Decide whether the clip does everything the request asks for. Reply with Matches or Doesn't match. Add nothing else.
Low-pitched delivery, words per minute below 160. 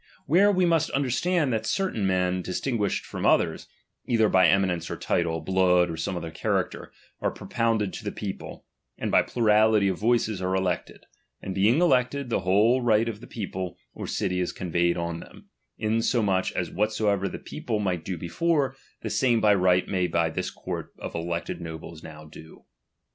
Doesn't match